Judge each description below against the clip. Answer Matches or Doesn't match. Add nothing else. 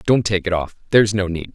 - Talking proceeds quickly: Matches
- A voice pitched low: Matches